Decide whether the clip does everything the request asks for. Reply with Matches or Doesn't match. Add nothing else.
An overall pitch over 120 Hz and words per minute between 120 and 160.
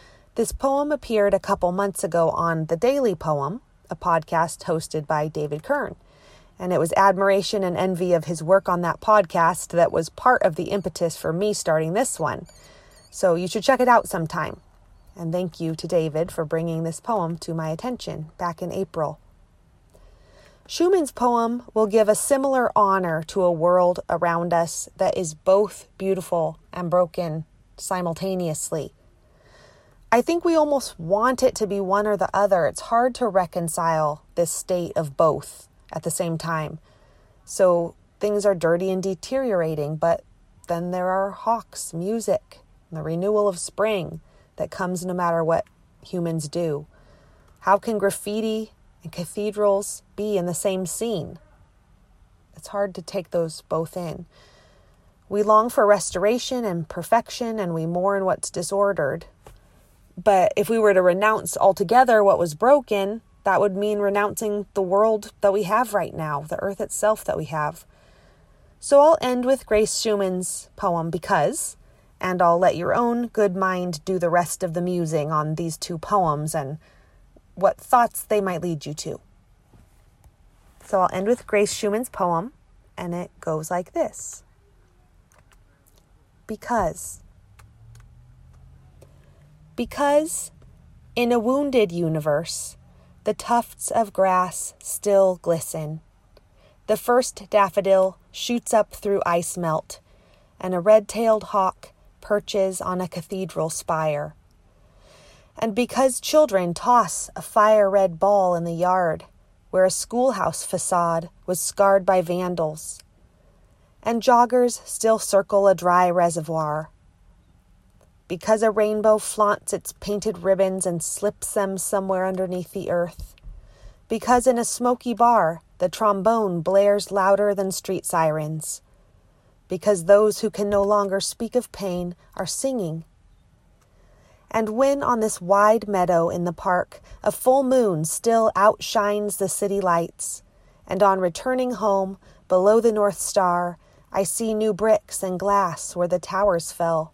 Matches